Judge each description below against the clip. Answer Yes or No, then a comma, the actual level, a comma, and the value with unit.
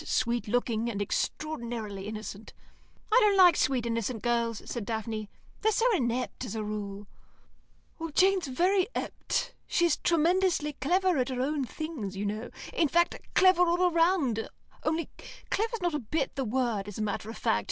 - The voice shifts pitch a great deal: Yes, wide, 7.7 semitones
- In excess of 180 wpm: No, average, 165 wpm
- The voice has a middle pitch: No, very high, 255 Hz